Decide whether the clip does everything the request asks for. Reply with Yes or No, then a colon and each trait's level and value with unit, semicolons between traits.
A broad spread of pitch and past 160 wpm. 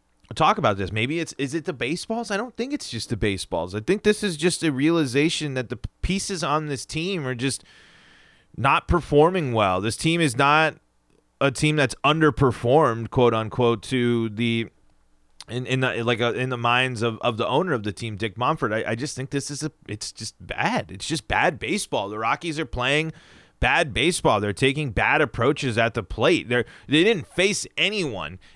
Yes: wide, 5.7 semitones; average, 200 wpm